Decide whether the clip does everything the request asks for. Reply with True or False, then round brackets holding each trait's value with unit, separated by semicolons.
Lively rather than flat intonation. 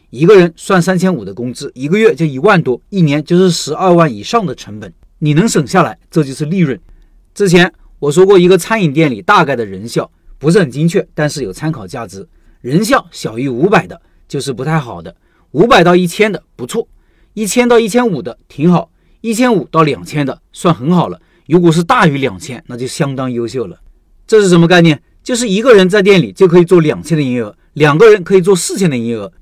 True (5.9 semitones)